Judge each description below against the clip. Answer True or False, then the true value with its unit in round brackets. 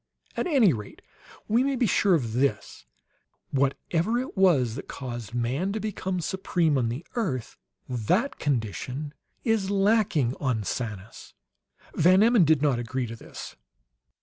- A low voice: False (150 Hz)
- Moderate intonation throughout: False (8.5 semitones)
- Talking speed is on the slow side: False (145 wpm)